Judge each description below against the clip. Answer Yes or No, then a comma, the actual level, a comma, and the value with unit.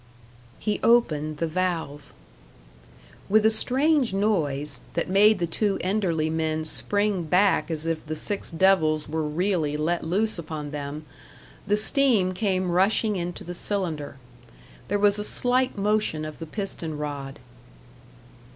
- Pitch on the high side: No, medium, 175 Hz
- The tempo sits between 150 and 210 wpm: No, average, 140 wpm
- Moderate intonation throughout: Yes, average, 4.9 semitones